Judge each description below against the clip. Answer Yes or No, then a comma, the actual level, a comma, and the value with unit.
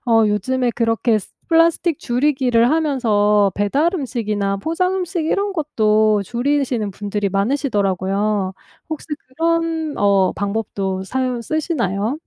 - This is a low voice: No, high, 235 Hz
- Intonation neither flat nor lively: No, wide, 6.6 semitones